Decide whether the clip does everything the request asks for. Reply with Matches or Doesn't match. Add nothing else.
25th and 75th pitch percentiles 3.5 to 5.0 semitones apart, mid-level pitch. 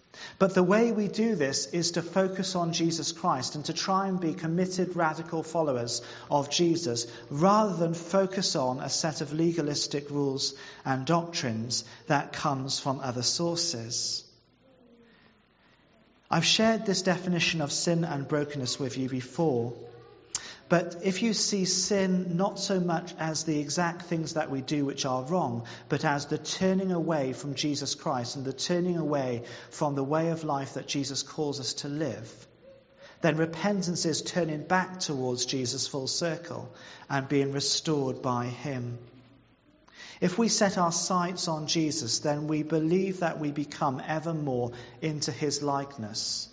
Matches